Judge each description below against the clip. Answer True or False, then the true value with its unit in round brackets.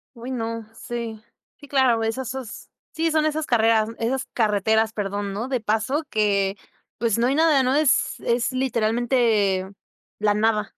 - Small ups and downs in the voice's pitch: False (3.3 semitones)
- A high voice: True (230 Hz)